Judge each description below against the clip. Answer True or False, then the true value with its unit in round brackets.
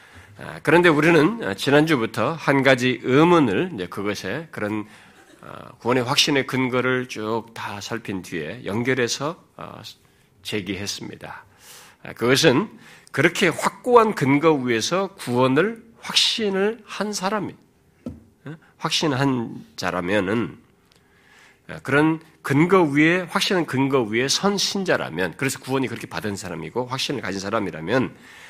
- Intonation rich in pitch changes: True (6.4 semitones)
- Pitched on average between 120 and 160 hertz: True (135 Hz)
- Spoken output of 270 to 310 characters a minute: False (255 characters per minute)